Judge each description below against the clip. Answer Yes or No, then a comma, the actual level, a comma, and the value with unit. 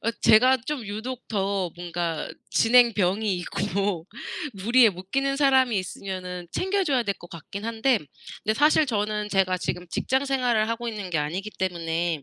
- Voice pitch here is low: No, high, 210 Hz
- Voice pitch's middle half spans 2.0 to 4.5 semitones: No, average, 5.3 semitones